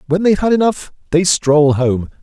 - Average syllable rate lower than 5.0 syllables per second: No, 5.1 syllables/s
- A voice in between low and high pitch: Yes, medium, 165 Hz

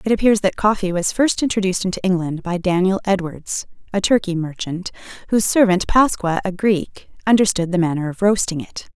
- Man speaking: No, female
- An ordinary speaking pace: Yes, average, 175 wpm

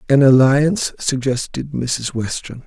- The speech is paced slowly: Yes, slow, 115 wpm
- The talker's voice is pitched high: No, low, 130 Hz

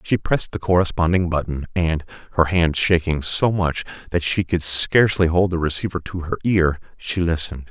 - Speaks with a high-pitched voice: No, very low, 85 Hz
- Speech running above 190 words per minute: No, average, 180 wpm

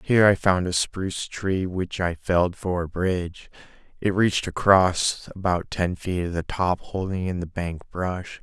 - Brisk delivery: No, average, 185 wpm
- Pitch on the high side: No, very low, 90 Hz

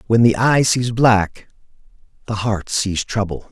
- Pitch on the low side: Yes, low, 110 Hz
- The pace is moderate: Yes, average, 155 wpm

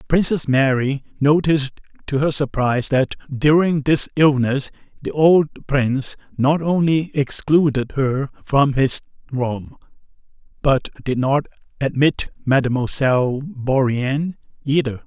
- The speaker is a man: Yes, male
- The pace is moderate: No, slow, 110 wpm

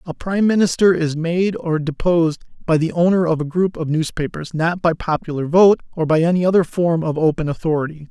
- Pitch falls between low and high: Yes, medium, 165 Hz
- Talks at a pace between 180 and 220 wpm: Yes, average, 200 wpm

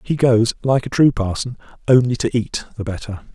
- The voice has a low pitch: Yes, low, 120 Hz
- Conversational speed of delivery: Yes, average, 195 wpm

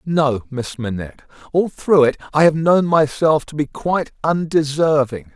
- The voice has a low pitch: No, medium, 145 Hz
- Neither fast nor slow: Yes, average, 155 wpm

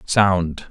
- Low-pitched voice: Yes, very low, 90 Hz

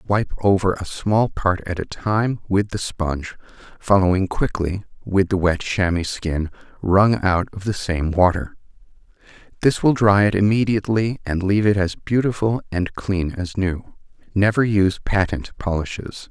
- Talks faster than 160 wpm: No, average, 155 wpm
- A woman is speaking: No, male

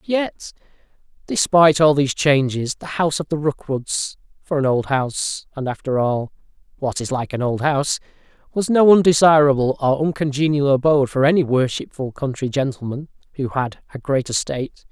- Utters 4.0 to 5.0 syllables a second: No, 5.3 syllables/s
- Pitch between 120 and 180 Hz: Yes, medium, 140 Hz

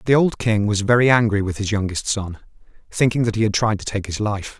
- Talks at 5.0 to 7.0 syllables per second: Yes, 5.8 syllables/s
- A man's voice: Yes, male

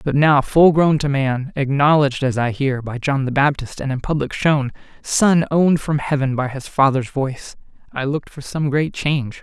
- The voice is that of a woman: No, male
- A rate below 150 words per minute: No, fast, 205 wpm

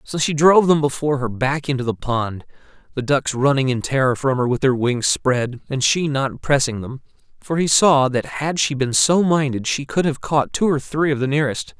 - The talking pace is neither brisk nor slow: No, fast, 230 wpm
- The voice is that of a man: Yes, male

